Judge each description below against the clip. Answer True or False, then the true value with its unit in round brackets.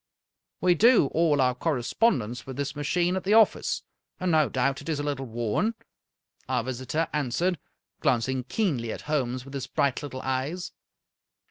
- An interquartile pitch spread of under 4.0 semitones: False (4.7 semitones)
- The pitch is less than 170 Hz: True (140 Hz)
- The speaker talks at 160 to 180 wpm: True (170 wpm)